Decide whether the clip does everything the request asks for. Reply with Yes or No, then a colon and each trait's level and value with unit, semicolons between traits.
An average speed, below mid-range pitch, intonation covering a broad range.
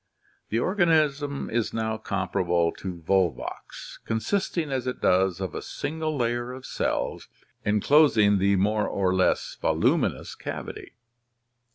No: slow, 125 wpm; low, 110 Hz; wide, 6.7 semitones